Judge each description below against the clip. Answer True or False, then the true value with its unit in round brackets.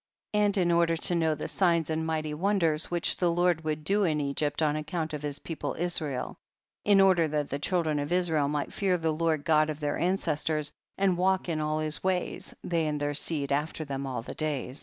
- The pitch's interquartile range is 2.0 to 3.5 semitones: True (2.7 semitones)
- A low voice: False (160 Hz)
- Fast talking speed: True (225 wpm)